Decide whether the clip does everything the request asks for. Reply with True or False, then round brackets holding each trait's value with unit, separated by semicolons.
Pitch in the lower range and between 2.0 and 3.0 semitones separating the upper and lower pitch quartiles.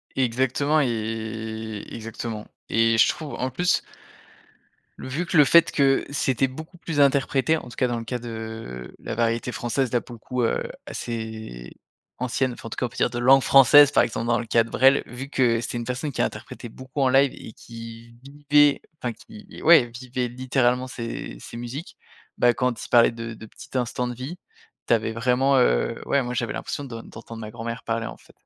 True (120 Hz; 2.7 semitones)